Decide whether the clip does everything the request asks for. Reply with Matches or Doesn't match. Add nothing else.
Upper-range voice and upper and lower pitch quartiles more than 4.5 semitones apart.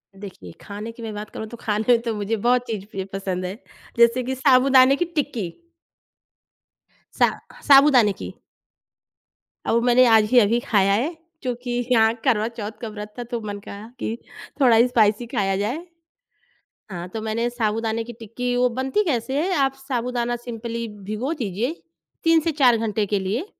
Doesn't match